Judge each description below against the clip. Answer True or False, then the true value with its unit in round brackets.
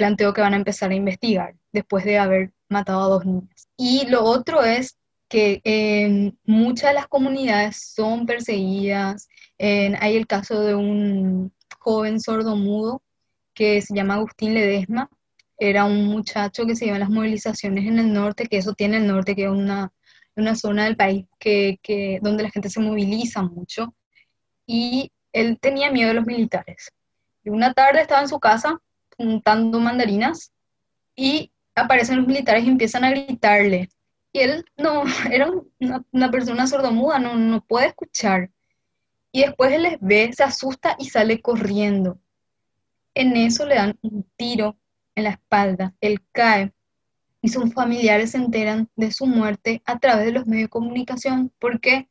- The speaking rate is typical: True (165 wpm)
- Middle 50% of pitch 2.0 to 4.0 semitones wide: True (3.6 semitones)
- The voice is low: False (220 Hz)